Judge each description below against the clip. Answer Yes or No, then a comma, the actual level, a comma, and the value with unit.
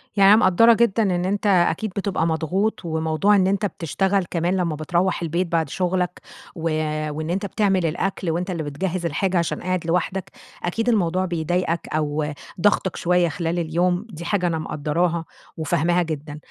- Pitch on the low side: No, medium, 175 Hz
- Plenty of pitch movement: No, average, 2.7 semitones